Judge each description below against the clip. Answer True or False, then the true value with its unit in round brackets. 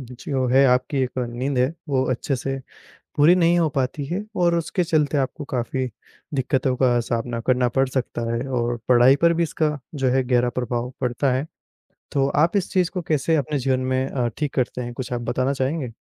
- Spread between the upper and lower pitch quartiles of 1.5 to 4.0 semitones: True (3.0 semitones)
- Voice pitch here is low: True (130 Hz)